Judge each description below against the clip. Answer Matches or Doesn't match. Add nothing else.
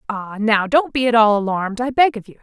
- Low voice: Doesn't match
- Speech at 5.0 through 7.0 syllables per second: Matches